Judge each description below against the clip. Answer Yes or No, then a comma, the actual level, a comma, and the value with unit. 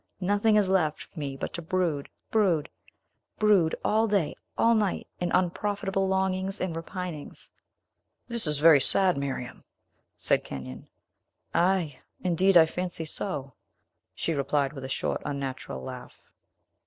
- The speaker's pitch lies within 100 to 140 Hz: No, medium, 175 Hz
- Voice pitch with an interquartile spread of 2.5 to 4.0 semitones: No, average, 4.7 semitones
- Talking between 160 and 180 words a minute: No, slow, 135 wpm